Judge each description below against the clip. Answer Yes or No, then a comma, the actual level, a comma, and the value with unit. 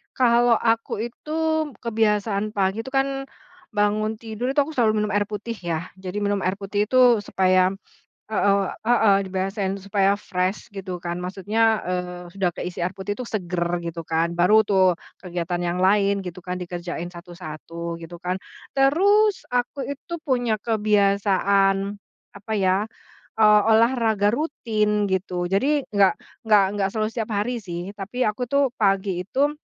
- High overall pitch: Yes, high, 205 Hz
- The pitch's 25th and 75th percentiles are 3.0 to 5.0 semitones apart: Yes, average, 3.6 semitones